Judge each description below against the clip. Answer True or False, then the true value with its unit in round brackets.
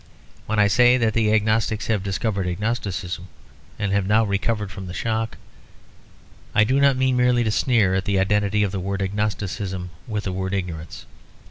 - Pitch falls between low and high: False (105 Hz)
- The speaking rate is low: False (175 wpm)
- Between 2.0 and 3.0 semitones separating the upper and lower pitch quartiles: True (2.6 semitones)